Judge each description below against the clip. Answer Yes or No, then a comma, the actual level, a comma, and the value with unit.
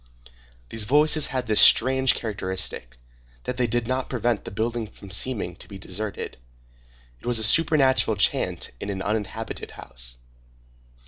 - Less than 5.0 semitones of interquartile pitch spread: Yes, average, 4.4 semitones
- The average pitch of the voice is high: No, low, 110 Hz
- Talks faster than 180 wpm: No, average, 145 wpm